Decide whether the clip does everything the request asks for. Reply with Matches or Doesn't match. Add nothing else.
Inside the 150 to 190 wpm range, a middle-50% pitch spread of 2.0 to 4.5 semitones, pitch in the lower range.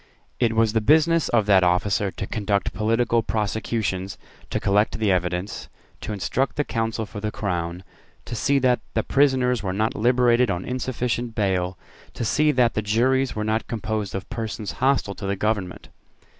Matches